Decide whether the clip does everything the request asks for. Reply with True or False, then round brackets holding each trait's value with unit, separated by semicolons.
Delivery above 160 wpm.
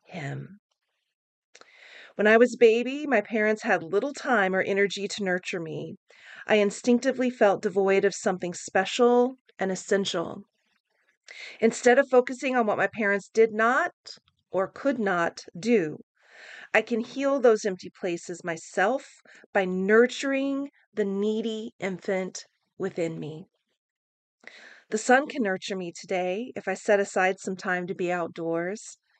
False (135 wpm)